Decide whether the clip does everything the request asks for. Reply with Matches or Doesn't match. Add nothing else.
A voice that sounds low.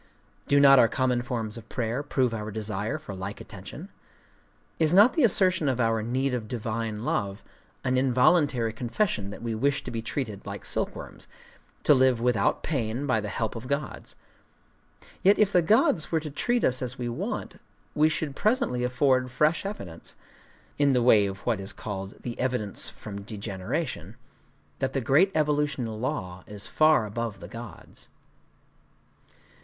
Matches